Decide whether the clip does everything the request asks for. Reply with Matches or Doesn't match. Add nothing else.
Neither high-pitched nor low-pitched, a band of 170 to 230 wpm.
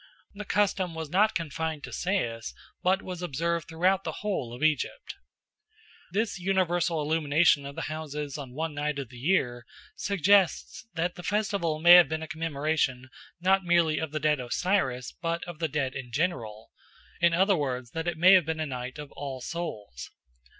Matches